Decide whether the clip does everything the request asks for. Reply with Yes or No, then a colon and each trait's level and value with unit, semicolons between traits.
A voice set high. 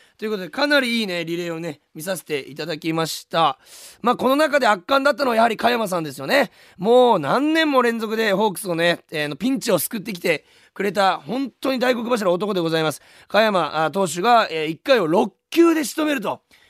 Yes: high, 215 Hz